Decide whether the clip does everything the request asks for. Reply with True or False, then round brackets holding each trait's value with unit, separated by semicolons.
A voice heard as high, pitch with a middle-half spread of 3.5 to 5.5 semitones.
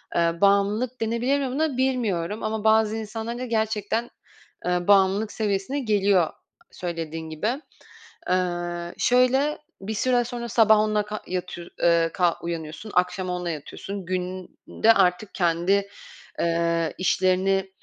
True (200 Hz; 4.0 semitones)